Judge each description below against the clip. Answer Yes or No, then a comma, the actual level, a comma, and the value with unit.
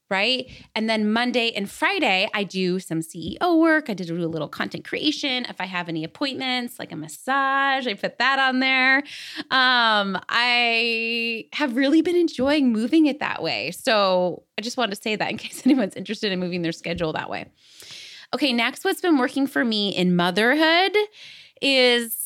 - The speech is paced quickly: No, average, 180 wpm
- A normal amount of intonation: No, wide, 6.5 semitones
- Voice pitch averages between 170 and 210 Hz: No, high, 235 Hz